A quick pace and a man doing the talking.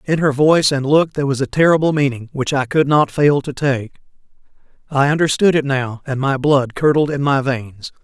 Yes: fast, 210 wpm; male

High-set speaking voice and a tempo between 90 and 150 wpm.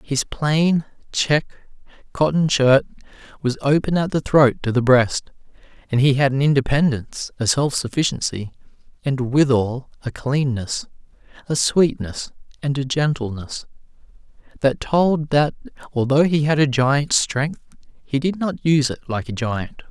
No: medium, 140 Hz; average, 140 wpm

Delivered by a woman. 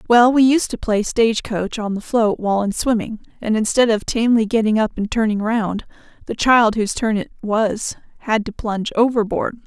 Yes: female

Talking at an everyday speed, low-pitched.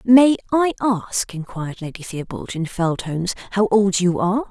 No: average, 175 wpm; high, 200 Hz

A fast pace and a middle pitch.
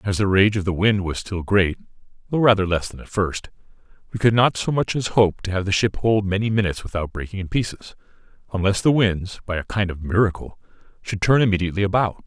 No: fast, 220 wpm; low, 100 Hz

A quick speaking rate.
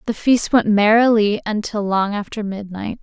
No: average, 160 wpm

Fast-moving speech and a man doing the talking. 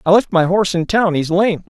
Yes: fast, 240 wpm; male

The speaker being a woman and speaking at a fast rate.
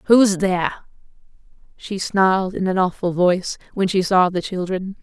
No: female; average, 155 wpm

